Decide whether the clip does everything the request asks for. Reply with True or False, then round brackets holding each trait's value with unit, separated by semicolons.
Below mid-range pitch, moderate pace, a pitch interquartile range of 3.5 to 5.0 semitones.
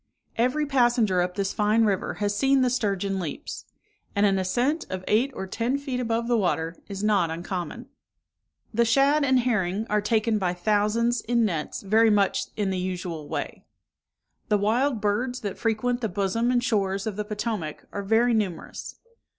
False (210 Hz; 175 wpm; 3.8 semitones)